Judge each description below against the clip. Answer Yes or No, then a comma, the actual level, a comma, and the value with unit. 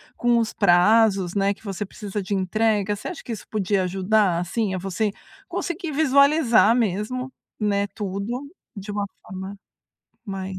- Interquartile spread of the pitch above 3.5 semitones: No, average, 3.0 semitones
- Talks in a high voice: Yes, high, 205 Hz